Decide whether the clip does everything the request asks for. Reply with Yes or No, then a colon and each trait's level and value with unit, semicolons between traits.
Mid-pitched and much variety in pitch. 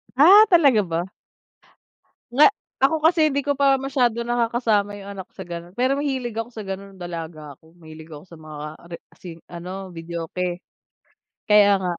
No: high, 195 Hz; wide, 7.0 semitones